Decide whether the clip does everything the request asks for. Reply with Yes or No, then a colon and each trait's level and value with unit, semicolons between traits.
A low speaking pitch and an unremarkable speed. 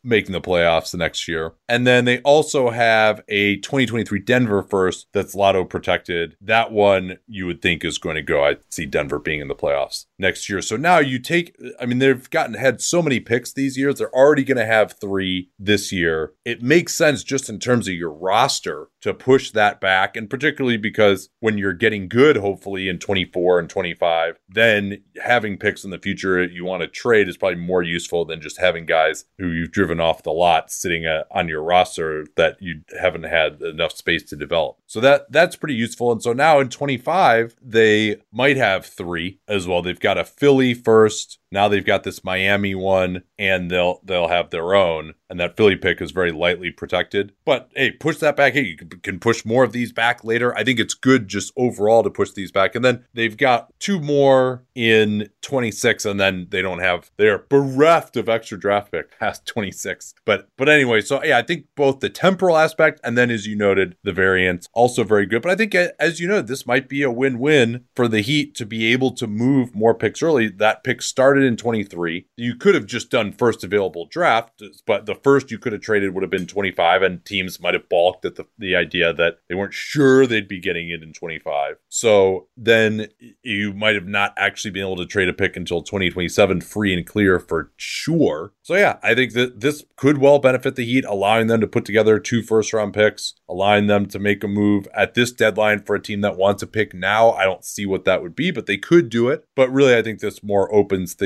No: low, 110 Hz; fast, 220 wpm